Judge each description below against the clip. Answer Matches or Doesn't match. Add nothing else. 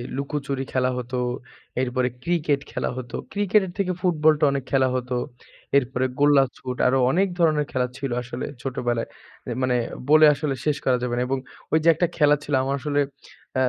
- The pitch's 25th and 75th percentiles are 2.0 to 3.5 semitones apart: Matches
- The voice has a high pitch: Doesn't match